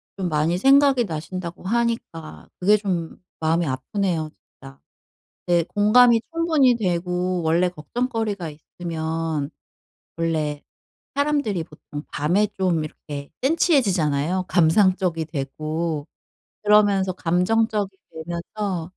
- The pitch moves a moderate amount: Yes, average, 4.7 semitones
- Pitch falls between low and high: Yes, medium, 180 Hz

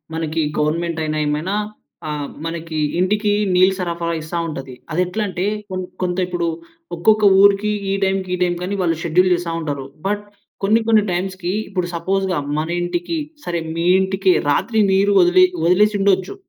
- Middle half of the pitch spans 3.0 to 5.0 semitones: No, narrow, 2.5 semitones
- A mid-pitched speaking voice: Yes, medium, 180 Hz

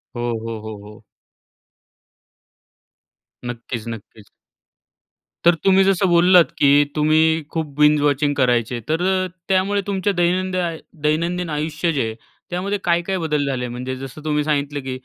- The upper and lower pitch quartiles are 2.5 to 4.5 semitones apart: No, average, 5.1 semitones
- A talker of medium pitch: Yes, medium, 155 Hz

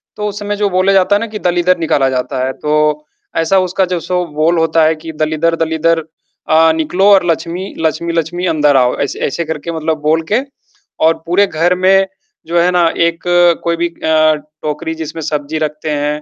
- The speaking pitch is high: No, medium, 165 Hz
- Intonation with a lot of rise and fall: No, narrow, 2.5 semitones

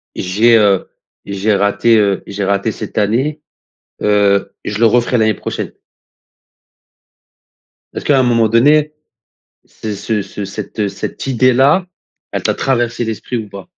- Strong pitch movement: No, average, 3.3 semitones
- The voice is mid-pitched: No, low, 110 Hz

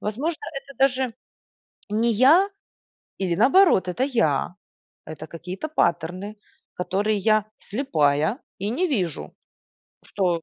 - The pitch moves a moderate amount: No, wide, 6.8 semitones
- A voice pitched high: Yes, high, 210 Hz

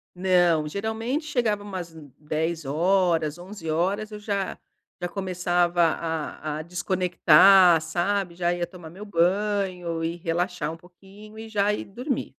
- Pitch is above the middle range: No, medium, 180 Hz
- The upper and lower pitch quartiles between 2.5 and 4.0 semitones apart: Yes, average, 3.3 semitones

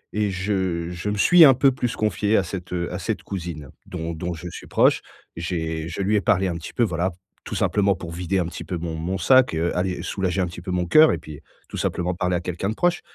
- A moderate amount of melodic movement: Yes, average, 3.0 semitones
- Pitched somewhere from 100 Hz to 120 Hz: No, very low, 90 Hz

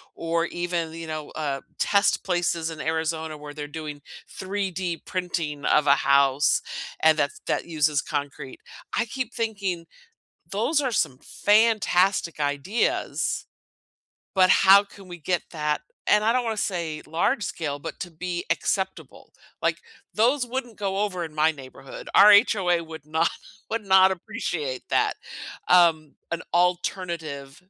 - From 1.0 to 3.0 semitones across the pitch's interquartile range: No, average, 4.3 semitones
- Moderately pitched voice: Yes, medium, 170 Hz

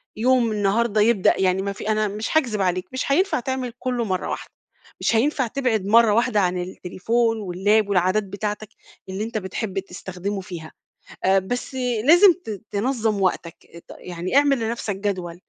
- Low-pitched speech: No, high, 210 Hz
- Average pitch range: Yes, average, 3.7 semitones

